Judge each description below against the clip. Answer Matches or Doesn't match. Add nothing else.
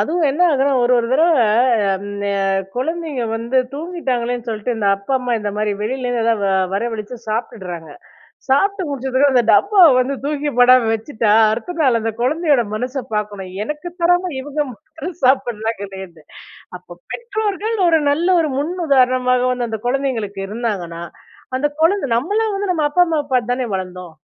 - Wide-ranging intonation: Matches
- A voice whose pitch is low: Doesn't match